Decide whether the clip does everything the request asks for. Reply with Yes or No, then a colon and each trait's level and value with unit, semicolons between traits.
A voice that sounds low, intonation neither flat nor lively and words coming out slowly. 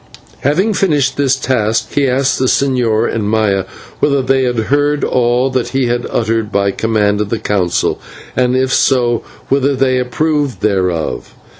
No: low, 125 Hz; average, 3.6 semitones; average, 160 wpm